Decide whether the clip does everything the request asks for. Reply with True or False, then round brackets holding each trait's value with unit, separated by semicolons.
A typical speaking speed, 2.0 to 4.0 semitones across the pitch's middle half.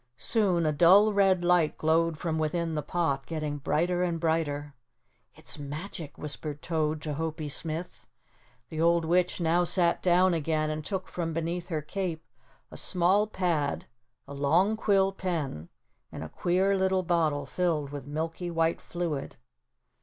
True (155 wpm; 2.7 semitones)